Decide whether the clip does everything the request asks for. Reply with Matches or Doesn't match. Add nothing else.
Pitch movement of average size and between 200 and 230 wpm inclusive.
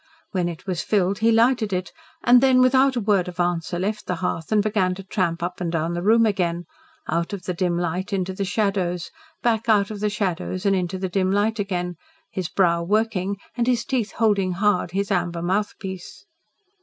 Matches